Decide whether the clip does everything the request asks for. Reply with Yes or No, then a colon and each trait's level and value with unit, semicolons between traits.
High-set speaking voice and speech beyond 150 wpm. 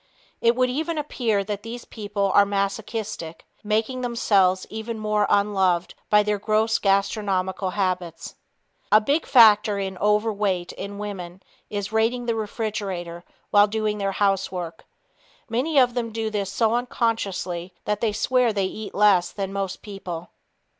No: high, 210 Hz; average, 145 wpm